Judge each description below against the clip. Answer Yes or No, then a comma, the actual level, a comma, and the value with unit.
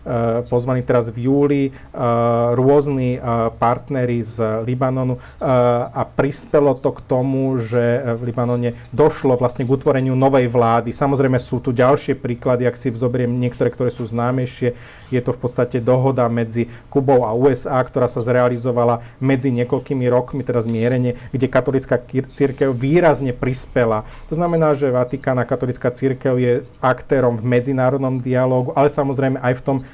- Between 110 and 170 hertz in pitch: Yes, low, 125 Hz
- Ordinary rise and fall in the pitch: No, narrow, 1.8 semitones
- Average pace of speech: Yes, average, 145 wpm